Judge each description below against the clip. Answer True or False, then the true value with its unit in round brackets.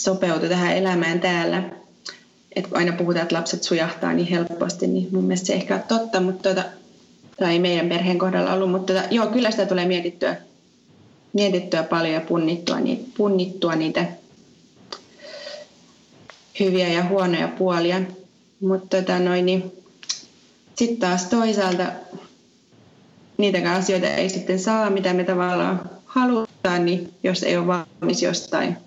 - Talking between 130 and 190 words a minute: True (135 wpm)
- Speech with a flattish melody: True (1.5 semitones)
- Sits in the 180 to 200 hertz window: True (185 Hz)